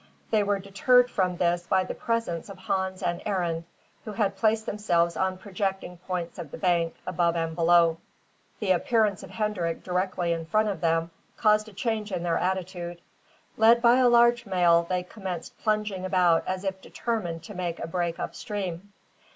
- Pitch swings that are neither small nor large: Yes, average, 3.5 semitones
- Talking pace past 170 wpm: Yes, average, 180 wpm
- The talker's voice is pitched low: No, medium, 185 Hz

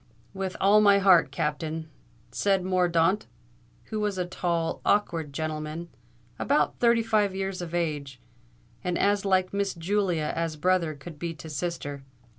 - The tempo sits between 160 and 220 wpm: No, average, 145 wpm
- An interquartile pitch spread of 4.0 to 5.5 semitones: No, average, 3.5 semitones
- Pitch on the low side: No, medium, 175 Hz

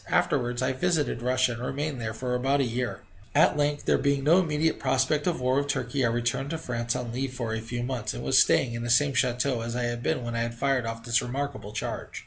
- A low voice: Yes, low, 125 Hz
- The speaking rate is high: Yes, fast, 250 wpm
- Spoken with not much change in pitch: No, average, 3.0 semitones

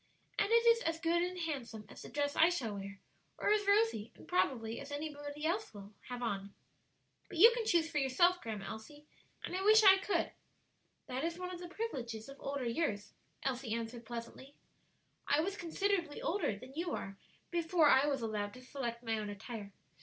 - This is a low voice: No, very high, 285 Hz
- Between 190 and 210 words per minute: Yes, average, 195 wpm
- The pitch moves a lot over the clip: Yes, wide, 7.4 semitones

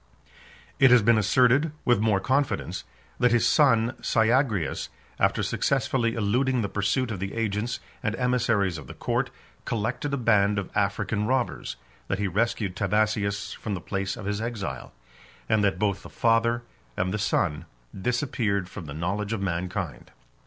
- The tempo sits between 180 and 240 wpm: No, average, 160 wpm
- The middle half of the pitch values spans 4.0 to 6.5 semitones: No, average, 3.3 semitones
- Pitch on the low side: Yes, low, 105 Hz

